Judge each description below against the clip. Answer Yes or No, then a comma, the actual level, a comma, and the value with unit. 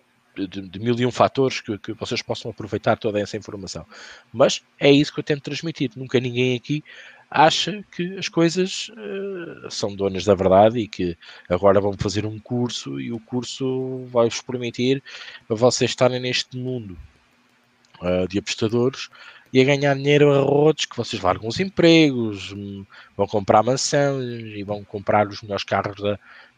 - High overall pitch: No, low, 120 Hz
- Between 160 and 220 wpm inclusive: Yes, average, 170 wpm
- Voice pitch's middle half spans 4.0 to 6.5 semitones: Yes, average, 4.8 semitones